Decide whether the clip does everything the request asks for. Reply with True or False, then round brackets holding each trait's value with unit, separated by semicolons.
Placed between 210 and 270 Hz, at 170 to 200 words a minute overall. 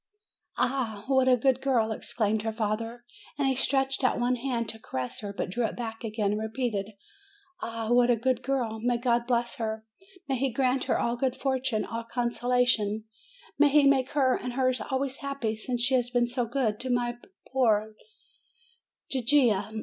True (240 Hz; 180 wpm)